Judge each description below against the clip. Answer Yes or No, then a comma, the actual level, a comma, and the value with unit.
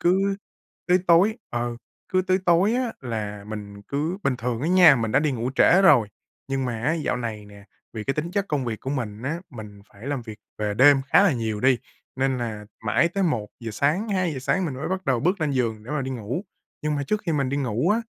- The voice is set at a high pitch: No, low, 135 Hz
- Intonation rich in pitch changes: Yes, wide, 6.9 semitones